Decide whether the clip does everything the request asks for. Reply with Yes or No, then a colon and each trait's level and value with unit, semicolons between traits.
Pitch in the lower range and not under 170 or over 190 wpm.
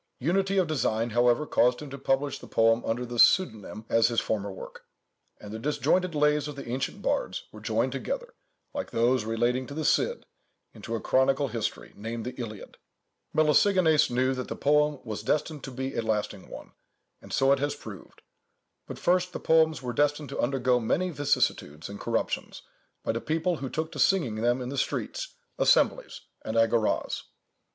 Yes: low, 130 Hz; average, 185 wpm